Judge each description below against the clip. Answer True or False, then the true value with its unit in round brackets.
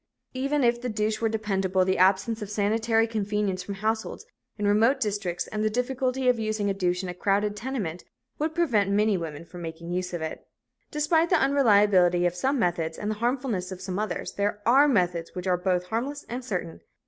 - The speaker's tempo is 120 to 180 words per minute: False (195 wpm)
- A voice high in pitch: True (210 Hz)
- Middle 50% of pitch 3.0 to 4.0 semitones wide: False (4.5 semitones)